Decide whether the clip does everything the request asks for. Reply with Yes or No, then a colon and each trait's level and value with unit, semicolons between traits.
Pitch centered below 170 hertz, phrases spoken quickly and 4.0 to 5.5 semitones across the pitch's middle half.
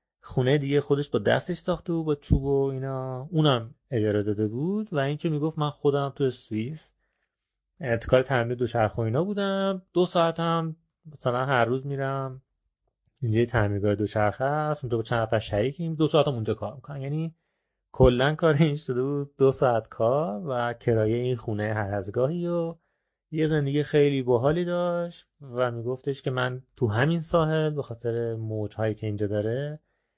Yes: low, 135 Hz; fast, 165 wpm; average, 4.8 semitones